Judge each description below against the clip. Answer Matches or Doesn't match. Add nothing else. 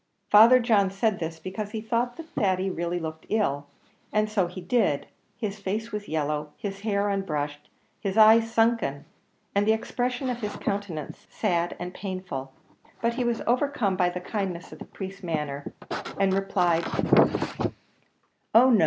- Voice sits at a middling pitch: Doesn't match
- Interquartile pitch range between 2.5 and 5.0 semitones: Matches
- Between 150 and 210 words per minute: Matches